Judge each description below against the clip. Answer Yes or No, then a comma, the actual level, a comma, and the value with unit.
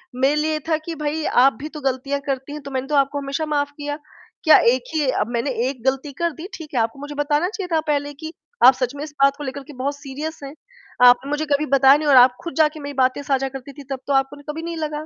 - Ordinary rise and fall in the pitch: No, narrow, 2.0 semitones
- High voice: Yes, very high, 285 Hz